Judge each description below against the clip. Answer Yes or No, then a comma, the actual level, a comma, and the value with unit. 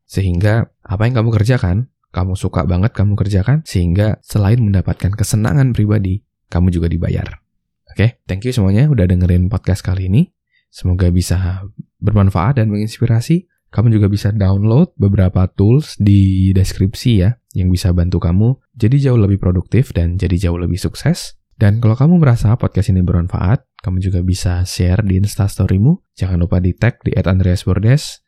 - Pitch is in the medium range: No, low, 100 Hz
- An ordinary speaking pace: No, fast, 155 wpm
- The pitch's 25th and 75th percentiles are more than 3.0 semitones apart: Yes, average, 3.7 semitones